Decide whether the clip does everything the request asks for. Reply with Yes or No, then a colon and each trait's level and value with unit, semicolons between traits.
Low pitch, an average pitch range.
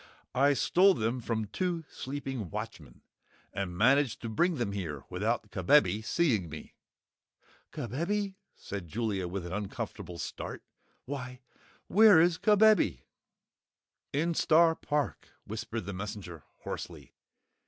No: low, 115 Hz; wide, 8.6 semitones